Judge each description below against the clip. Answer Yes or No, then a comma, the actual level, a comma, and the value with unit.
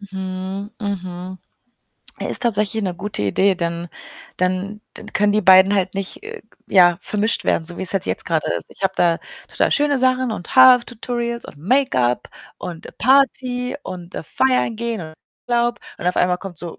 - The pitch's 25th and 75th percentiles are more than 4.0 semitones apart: Yes, average, 4.8 semitones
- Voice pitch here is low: No, high, 195 Hz